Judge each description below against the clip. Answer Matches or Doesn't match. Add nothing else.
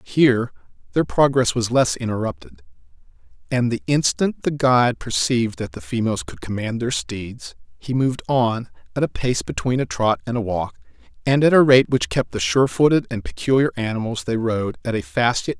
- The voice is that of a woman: Doesn't match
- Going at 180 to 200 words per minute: Matches